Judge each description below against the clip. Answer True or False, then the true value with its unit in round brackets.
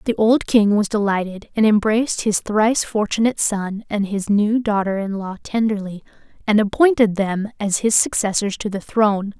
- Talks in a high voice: True (210 Hz)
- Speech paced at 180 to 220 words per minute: False (170 wpm)